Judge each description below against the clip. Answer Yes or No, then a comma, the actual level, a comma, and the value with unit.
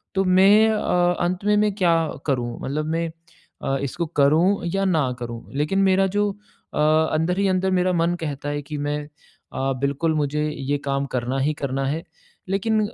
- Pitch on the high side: No, medium, 160 Hz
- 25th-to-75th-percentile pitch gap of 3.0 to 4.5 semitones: No, average, 4.9 semitones